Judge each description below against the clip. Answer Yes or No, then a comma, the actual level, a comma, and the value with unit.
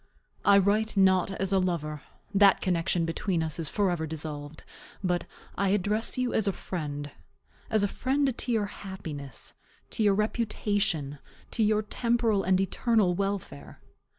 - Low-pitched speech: No, high, 195 Hz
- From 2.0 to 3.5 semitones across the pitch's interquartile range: No, average, 4.3 semitones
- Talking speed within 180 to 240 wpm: No, average, 150 wpm